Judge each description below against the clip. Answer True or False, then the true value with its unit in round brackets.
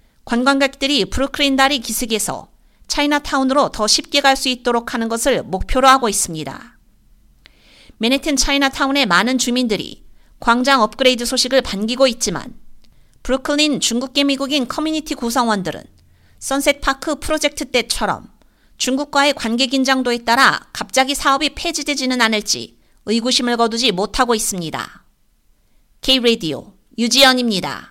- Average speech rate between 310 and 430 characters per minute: True (335 characters per minute)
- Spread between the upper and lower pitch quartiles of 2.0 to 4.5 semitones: True (3.3 semitones)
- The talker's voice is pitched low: False (260 Hz)